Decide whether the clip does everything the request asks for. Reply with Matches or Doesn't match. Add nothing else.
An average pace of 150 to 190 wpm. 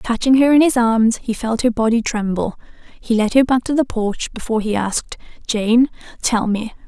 Doesn't match